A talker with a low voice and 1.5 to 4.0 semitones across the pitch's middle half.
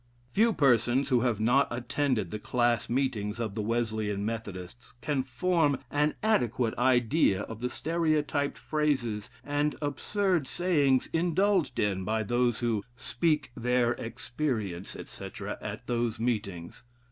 No: low, 125 Hz; average, 4.7 semitones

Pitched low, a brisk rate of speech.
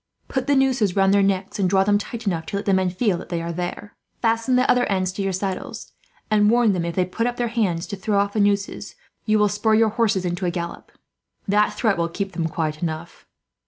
No: high, 200 Hz; fast, 245 wpm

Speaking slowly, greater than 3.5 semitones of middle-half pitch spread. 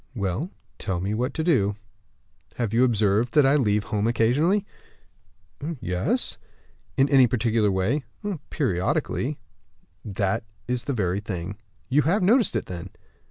Yes: slow, 130 wpm; wide, 5.4 semitones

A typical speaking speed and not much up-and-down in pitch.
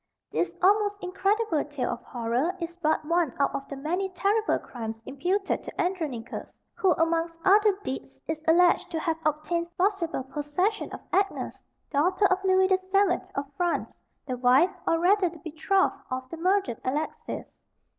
No: average, 160 wpm; average, 4.6 semitones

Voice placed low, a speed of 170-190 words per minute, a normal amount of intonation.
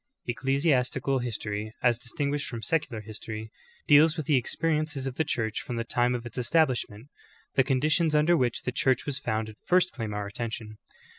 Yes: low, 125 Hz; average, 175 wpm; average, 4.5 semitones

